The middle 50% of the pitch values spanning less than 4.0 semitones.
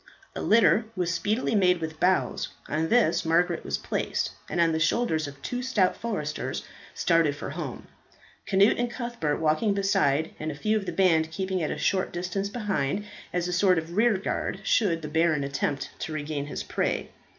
No: average, 4.3 semitones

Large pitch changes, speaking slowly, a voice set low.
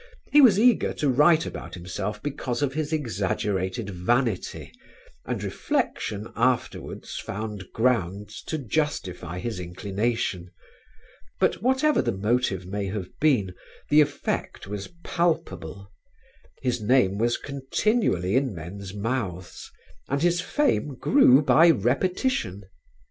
Yes: wide, 7.3 semitones; slow, 115 wpm; low, 115 Hz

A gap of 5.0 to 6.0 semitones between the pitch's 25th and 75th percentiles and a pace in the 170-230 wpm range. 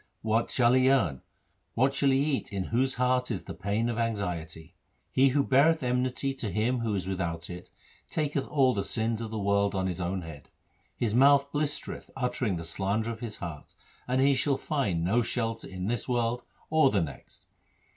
Yes: average, 5.3 semitones; average, 195 wpm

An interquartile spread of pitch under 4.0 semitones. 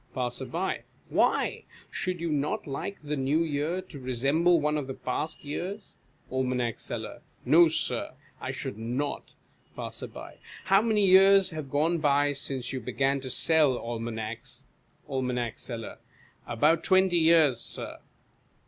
No: average, 4.5 semitones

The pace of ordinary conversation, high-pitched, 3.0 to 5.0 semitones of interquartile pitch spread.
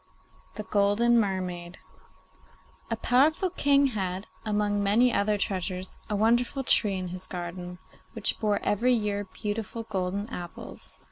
No: slow, 130 wpm; high, 205 Hz; average, 3.5 semitones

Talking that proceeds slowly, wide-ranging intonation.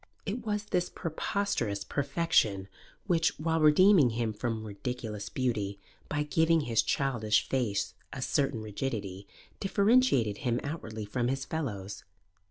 Yes: slow, 125 wpm; wide, 7.3 semitones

